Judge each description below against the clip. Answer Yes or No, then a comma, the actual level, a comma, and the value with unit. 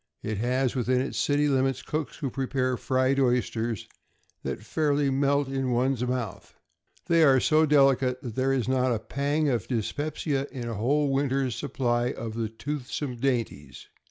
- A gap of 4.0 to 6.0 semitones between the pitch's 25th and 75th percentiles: No, narrow, 2.4 semitones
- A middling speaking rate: Yes, average, 160 wpm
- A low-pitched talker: Yes, low, 130 Hz